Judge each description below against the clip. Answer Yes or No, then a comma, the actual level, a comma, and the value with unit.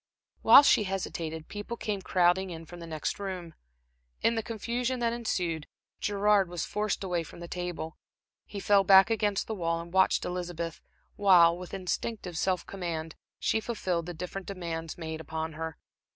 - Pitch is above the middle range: No, medium, 180 Hz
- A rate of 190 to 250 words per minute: No, average, 165 wpm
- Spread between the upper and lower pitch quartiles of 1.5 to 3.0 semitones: No, average, 3.4 semitones